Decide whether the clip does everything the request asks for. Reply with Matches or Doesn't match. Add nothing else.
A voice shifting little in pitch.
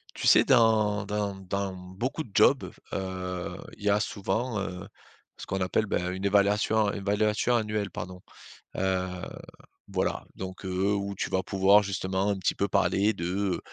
Matches